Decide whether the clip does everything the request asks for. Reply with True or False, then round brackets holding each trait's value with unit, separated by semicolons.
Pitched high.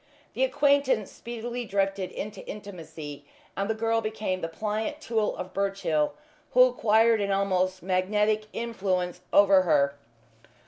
True (200 Hz)